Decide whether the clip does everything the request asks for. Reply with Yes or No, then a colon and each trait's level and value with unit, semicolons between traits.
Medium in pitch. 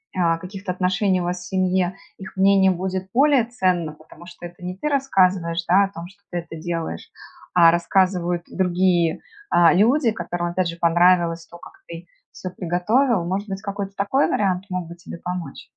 Yes: medium, 180 Hz